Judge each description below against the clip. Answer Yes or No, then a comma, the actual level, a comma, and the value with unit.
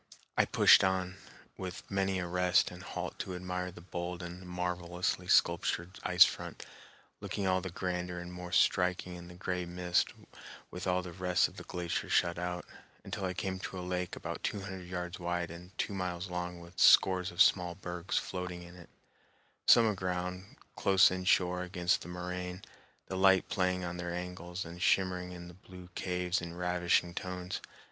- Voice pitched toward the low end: Yes, very low, 90 Hz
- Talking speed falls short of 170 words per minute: No, average, 180 wpm